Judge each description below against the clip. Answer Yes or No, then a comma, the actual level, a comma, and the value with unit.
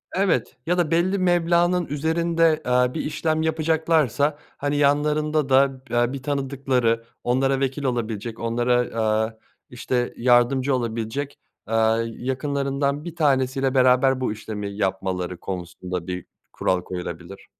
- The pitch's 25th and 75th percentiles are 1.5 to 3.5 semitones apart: No, average, 4.7 semitones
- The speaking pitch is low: Yes, low, 130 Hz